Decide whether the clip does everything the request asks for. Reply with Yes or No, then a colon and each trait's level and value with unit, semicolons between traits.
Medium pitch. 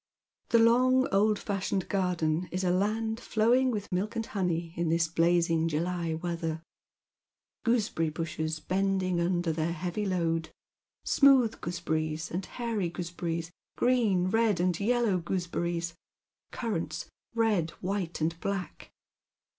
Yes: medium, 180 Hz